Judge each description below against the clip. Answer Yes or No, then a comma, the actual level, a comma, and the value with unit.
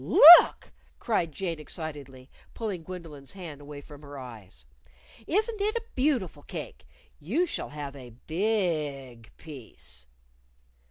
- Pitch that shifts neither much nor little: No, wide, 6.6 semitones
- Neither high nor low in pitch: Yes, medium, 155 Hz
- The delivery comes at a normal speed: No, slow, 130 wpm